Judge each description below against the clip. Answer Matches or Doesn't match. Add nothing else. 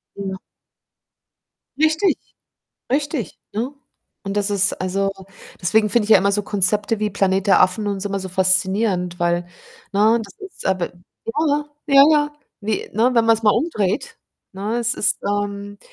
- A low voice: Doesn't match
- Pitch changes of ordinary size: Matches